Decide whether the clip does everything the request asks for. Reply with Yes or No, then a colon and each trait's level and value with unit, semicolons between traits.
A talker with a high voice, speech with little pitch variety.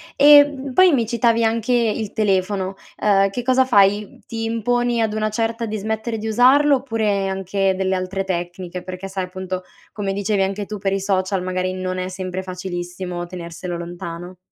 No: high, 195 Hz; average, 3.4 semitones